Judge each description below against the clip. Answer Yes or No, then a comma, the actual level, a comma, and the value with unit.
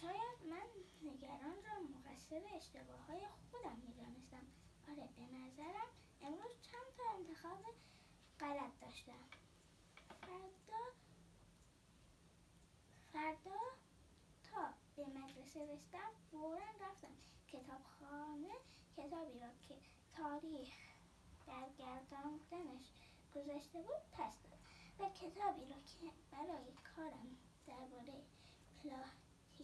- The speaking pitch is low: No, very high, 305 Hz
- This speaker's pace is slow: Yes, slow, 95 wpm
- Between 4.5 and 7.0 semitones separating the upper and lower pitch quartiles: Yes, average, 5.3 semitones